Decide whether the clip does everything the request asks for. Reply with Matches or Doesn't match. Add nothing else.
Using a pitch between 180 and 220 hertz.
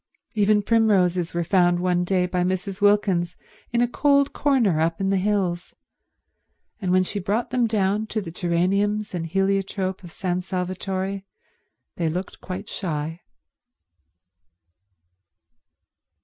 Matches